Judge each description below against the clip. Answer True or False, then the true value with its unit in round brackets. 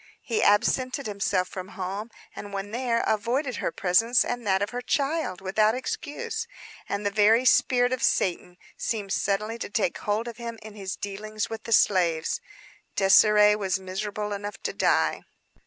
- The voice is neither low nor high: False (210 Hz)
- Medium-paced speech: True (165 wpm)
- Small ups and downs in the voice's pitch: False (3.1 semitones)